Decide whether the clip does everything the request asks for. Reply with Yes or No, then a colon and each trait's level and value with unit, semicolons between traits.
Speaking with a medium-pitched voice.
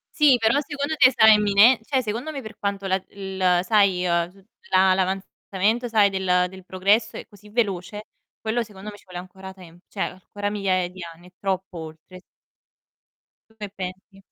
No: high, 195 Hz